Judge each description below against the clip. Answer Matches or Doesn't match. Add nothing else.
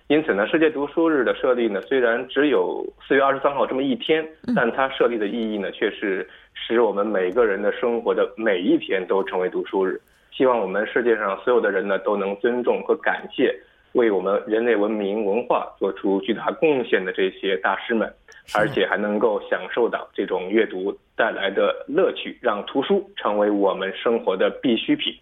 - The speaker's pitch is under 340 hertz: Doesn't match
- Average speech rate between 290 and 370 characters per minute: Matches